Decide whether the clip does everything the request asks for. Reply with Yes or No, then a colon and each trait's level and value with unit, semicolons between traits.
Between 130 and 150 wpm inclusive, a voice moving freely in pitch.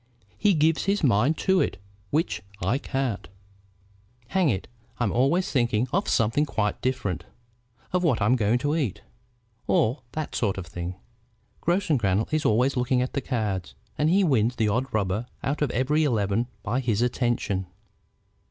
No: average, 160 wpm; wide, 5.8 semitones